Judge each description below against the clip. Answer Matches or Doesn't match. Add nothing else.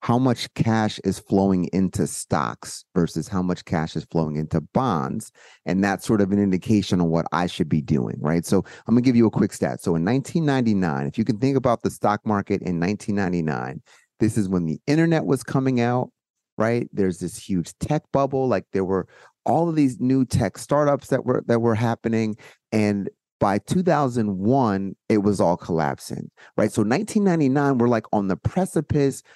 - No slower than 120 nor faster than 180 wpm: Doesn't match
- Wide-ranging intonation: Matches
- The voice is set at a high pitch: Doesn't match